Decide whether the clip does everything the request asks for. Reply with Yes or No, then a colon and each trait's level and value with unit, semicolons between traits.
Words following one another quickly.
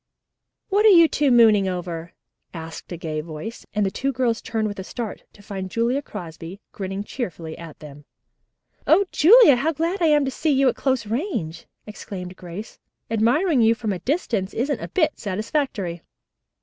No: average, 175 wpm